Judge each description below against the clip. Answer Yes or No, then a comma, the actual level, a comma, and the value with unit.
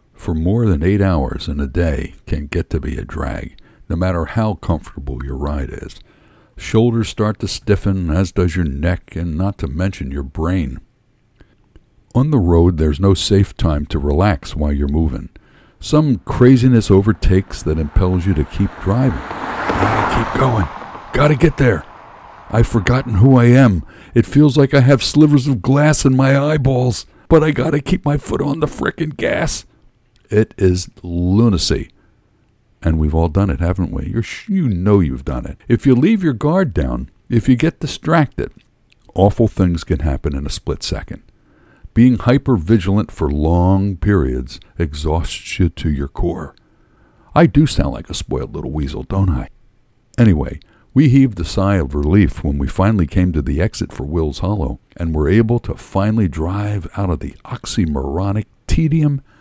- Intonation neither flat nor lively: No, wide, 6.6 semitones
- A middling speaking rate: Yes, average, 175 wpm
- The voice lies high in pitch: No, very low, 95 Hz